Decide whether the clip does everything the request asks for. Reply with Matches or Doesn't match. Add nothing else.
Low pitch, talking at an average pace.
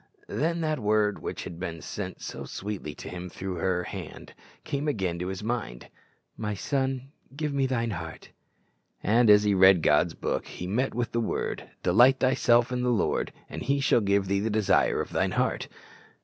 Matches